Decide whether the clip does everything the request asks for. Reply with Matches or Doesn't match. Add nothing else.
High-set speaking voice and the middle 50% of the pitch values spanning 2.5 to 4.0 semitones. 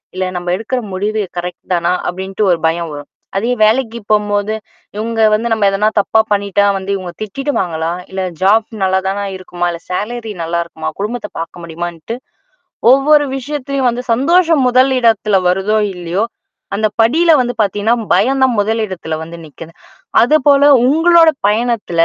Doesn't match